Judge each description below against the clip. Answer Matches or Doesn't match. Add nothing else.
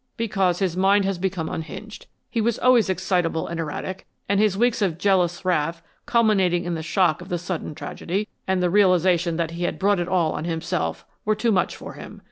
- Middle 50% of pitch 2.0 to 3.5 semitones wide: Matches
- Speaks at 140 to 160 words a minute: Doesn't match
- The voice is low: Doesn't match